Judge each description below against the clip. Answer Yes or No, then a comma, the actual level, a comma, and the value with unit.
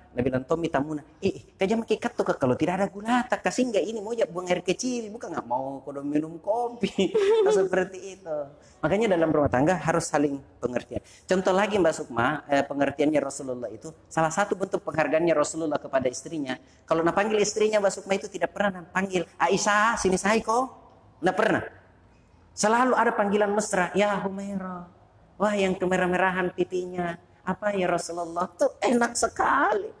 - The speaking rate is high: Yes, fast, 160 wpm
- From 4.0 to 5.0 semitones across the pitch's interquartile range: Yes, average, 4.5 semitones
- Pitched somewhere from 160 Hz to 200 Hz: Yes, medium, 185 Hz